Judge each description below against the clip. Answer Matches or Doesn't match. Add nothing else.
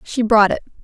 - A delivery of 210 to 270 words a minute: Matches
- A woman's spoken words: Matches